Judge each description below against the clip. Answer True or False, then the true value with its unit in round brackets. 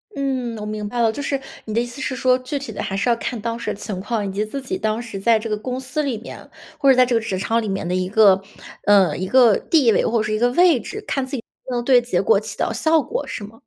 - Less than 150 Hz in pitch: False (230 Hz)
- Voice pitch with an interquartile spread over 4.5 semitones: False (3.5 semitones)